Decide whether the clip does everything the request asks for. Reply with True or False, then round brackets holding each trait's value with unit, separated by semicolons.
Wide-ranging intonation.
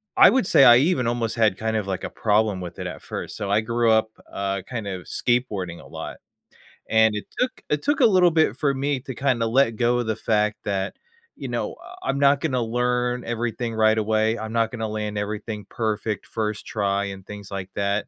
False (2.8 semitones)